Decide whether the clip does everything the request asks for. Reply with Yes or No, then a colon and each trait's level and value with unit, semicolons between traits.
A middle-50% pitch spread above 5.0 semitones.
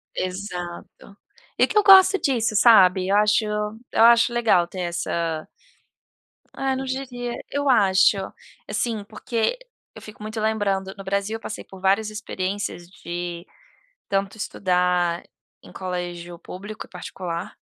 No: average, 3.7 semitones